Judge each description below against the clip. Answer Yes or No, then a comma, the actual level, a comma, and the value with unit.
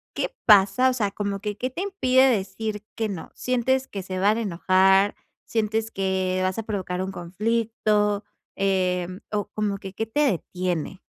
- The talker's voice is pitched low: No, high, 205 Hz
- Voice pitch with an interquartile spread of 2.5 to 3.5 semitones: Yes, average, 2.9 semitones